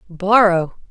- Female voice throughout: Yes, female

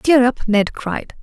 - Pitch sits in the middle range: No, high, 240 Hz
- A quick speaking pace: No, average, 195 wpm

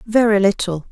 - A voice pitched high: Yes, high, 205 Hz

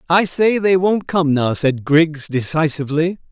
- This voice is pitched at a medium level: Yes, medium, 160 Hz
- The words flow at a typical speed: Yes, average, 165 wpm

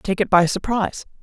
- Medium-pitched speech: No, high, 195 Hz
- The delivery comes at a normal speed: Yes, average, 195 wpm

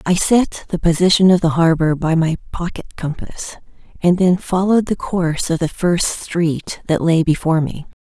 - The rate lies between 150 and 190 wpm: Yes, average, 180 wpm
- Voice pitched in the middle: Yes, medium, 170 Hz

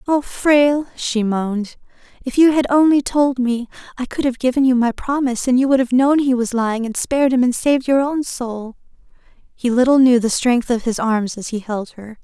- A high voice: Yes, very high, 250 Hz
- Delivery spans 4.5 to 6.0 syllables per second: Yes, 5.2 syllables/s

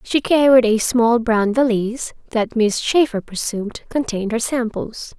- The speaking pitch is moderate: No, high, 230 Hz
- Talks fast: No, average, 150 wpm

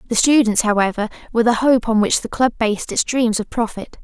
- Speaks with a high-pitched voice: Yes, high, 225 Hz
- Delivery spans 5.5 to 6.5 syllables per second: Yes, 6.0 syllables/s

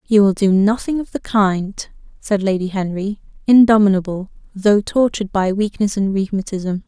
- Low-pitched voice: No, high, 200 Hz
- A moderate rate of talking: Yes, average, 150 wpm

